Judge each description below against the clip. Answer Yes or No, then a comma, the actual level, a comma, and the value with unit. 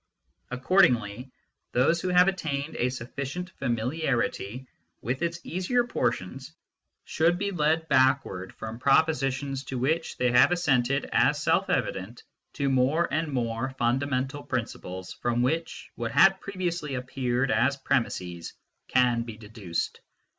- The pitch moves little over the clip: No, average, 5.0 semitones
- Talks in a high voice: No, low, 130 Hz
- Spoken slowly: Yes, slow, 125 wpm